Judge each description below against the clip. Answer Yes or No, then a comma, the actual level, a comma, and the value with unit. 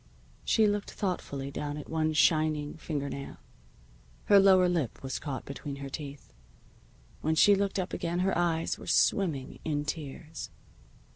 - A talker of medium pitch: Yes, medium, 155 Hz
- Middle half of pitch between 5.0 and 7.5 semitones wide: No, average, 4.0 semitones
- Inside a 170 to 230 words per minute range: No, average, 150 wpm